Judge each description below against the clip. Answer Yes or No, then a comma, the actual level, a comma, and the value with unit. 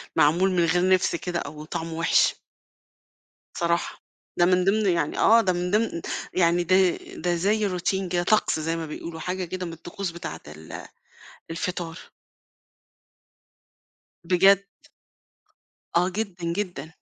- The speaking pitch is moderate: Yes, medium, 175 Hz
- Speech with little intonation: Yes, narrow, 2.0 semitones